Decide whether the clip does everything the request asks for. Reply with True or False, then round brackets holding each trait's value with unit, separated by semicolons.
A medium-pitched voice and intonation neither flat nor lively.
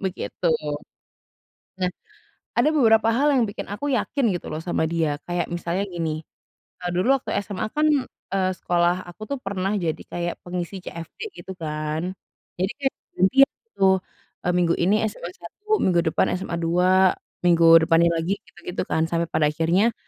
True (180 Hz; 3.2 semitones)